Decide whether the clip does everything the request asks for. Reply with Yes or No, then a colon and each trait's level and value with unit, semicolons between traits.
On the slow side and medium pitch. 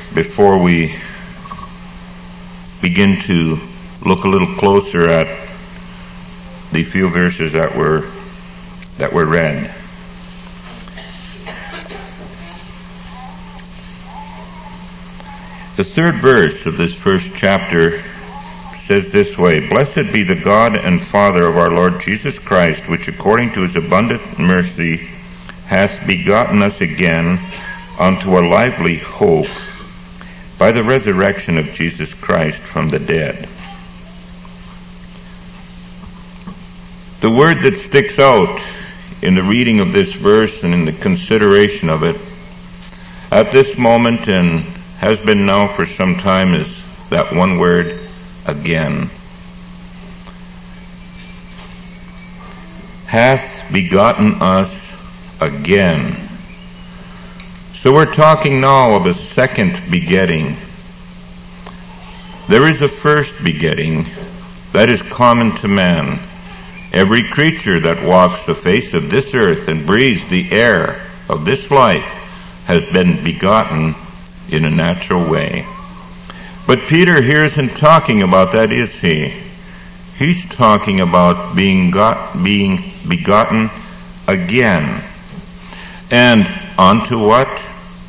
No: slow, 110 wpm; low, 115 Hz